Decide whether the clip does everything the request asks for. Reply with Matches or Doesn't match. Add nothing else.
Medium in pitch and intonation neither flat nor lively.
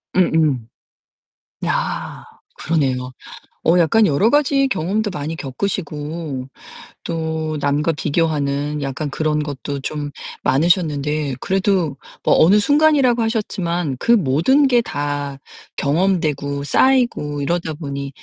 Matches